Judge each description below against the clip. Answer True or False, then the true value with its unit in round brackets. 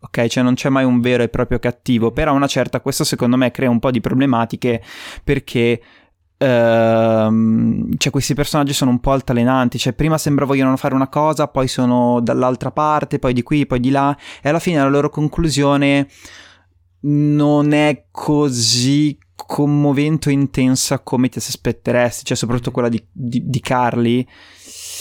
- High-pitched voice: False (130 Hz)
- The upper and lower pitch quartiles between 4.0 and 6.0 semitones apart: False (2.8 semitones)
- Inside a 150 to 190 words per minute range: True (165 wpm)